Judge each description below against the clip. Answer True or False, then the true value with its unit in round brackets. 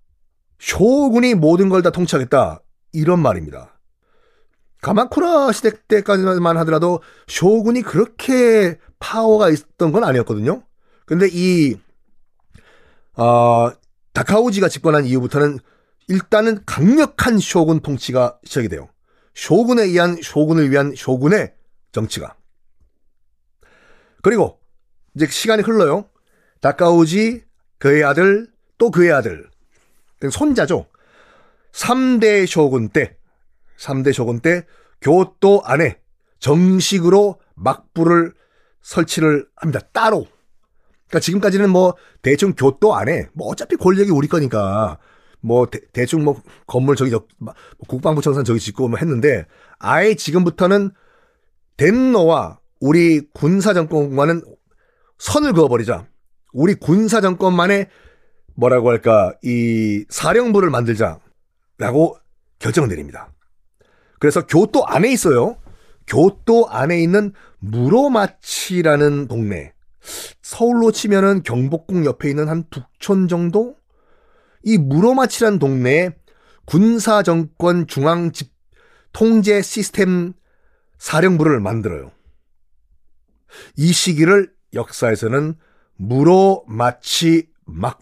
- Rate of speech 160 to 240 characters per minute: True (235 characters per minute)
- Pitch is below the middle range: False (170 Hz)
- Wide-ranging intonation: True (6.9 semitones)